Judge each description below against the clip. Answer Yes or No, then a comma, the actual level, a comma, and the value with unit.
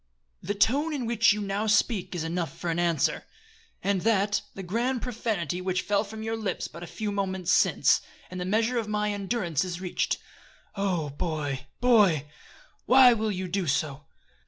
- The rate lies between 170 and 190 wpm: Yes, average, 180 wpm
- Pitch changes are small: No, average, 4.0 semitones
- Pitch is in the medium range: No, high, 200 Hz